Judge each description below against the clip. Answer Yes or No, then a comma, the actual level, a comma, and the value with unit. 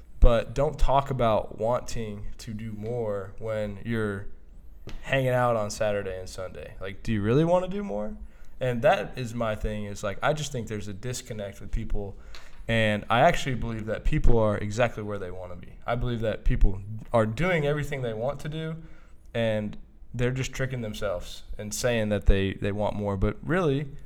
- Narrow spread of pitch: No, average, 3.6 semitones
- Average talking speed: Yes, average, 190 wpm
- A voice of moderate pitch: No, low, 110 Hz